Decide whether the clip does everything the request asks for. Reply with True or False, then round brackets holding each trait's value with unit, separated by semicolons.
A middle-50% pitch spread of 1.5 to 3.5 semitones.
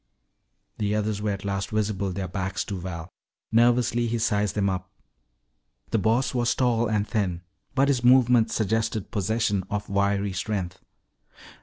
True (2.8 semitones)